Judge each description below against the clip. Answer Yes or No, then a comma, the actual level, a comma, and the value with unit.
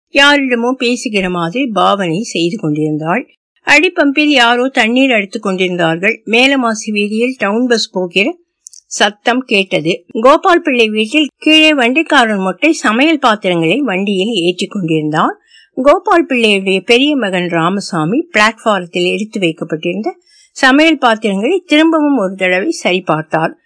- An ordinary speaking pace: Yes, average, 110 wpm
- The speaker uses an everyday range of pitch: No, wide, 7.0 semitones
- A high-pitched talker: Yes, high, 230 Hz